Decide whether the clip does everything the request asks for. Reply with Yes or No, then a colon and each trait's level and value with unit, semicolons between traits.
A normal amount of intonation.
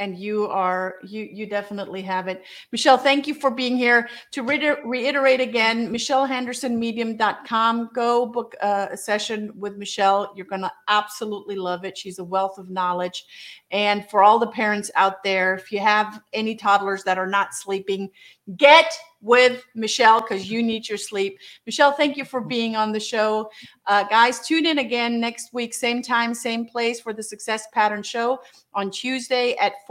Yes: average, 3.3 semitones